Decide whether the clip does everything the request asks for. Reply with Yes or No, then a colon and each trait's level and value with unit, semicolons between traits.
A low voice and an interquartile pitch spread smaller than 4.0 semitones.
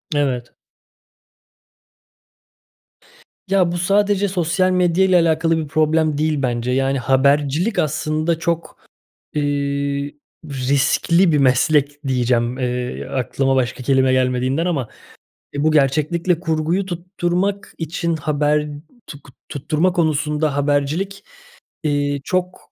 No: medium, 150 Hz; average, 3.6 semitones